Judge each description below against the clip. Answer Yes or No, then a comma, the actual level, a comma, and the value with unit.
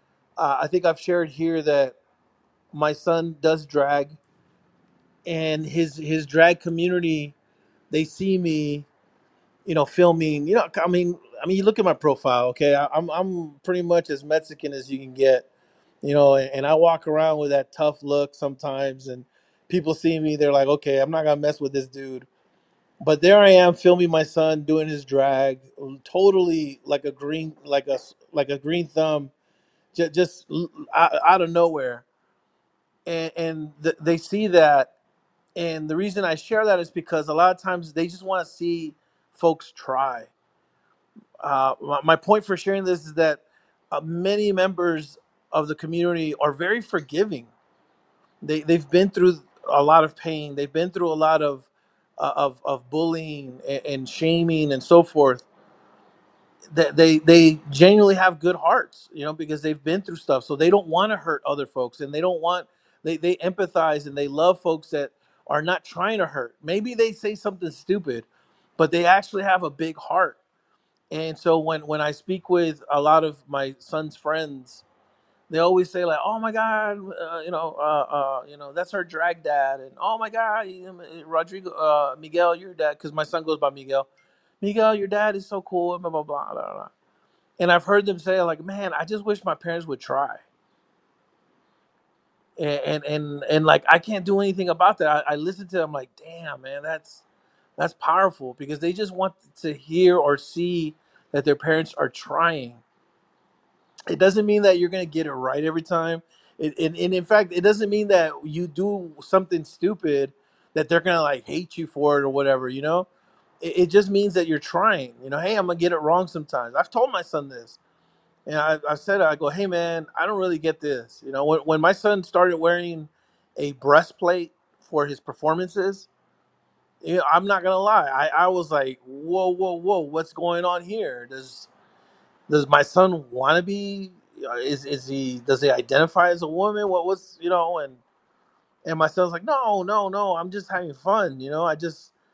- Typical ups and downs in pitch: Yes, average, 3.5 semitones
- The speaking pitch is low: No, medium, 165 Hz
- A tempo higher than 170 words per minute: Yes, average, 190 wpm